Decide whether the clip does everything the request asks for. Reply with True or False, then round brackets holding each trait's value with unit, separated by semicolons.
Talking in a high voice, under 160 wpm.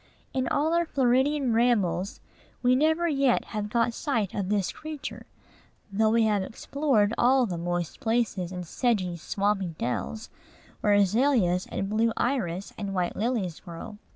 True (220 Hz; 150 wpm)